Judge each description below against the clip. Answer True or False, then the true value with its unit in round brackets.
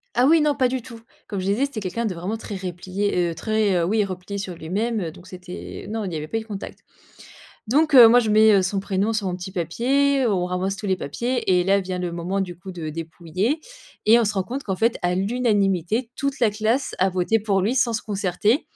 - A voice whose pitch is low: False (200 Hz)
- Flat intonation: False (4.0 semitones)